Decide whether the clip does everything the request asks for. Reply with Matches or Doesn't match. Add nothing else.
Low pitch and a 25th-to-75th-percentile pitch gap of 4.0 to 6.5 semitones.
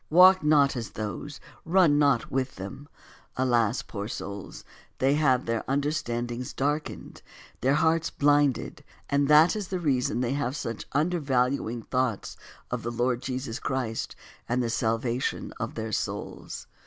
Doesn't match